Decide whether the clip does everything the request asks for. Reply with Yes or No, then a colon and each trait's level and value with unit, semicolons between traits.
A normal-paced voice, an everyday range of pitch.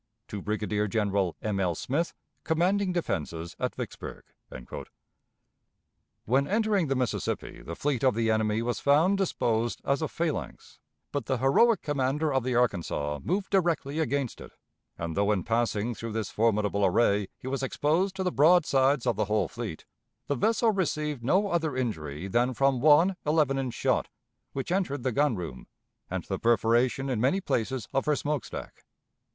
No: average, 170 wpm; wide, 5.9 semitones